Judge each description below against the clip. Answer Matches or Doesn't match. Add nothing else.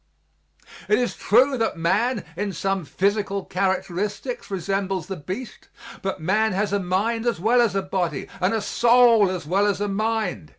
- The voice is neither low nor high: Doesn't match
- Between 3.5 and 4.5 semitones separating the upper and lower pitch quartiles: Doesn't match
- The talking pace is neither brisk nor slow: Matches